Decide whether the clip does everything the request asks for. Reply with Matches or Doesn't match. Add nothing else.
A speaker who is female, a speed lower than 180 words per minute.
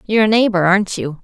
Doesn't match